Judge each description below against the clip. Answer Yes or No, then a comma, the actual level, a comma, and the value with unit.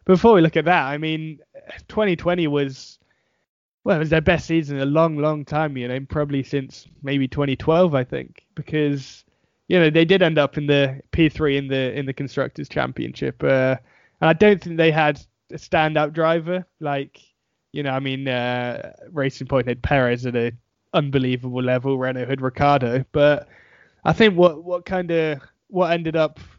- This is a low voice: No, medium, 145 Hz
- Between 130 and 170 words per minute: No, average, 185 wpm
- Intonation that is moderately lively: Yes, average, 3.6 semitones